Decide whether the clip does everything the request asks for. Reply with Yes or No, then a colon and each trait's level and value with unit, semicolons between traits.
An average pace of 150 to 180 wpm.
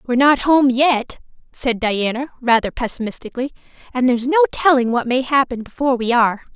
Yes: average, 165 wpm